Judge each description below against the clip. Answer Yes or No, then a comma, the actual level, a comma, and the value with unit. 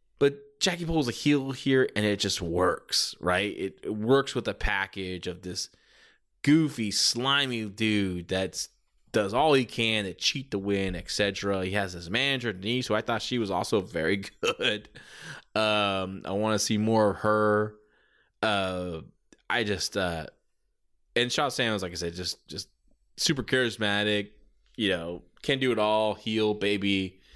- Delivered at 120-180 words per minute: Yes, average, 165 wpm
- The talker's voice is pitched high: No, low, 105 Hz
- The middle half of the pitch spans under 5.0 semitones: Yes, average, 4.0 semitones